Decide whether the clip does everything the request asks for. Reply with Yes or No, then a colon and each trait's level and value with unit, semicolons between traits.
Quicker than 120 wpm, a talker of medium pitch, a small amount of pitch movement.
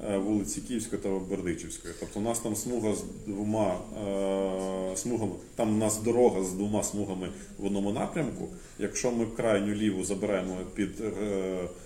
No: average, 140 wpm; low, 100 Hz; narrow, 2.2 semitones